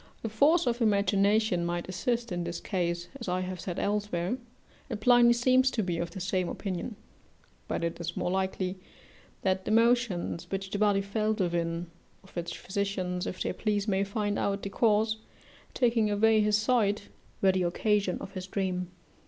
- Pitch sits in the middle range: No, high, 200 Hz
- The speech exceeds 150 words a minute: Yes, average, 175 wpm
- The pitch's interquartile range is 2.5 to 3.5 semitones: Yes, average, 3.2 semitones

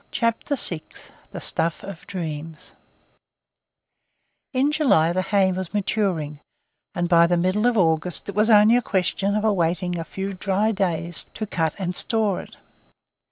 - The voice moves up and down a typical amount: Yes, average, 3.8 semitones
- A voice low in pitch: No, medium, 185 Hz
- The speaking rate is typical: Yes, average, 155 wpm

